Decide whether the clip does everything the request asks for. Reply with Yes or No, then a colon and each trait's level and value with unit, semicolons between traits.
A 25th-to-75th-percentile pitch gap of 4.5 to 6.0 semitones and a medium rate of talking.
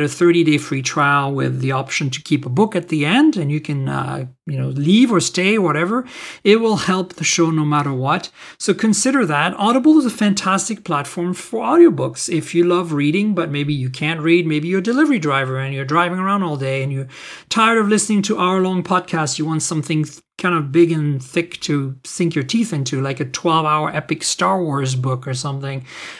No: average, 4.9 semitones; fast, 215 wpm